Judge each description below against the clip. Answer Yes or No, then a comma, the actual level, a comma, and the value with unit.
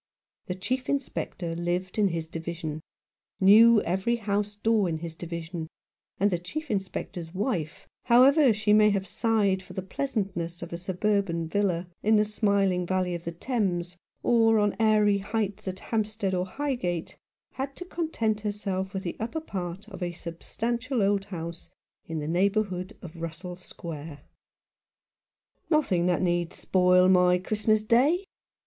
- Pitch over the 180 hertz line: Yes, high, 190 Hz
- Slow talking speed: No, average, 150 wpm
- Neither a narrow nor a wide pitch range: Yes, average, 3.7 semitones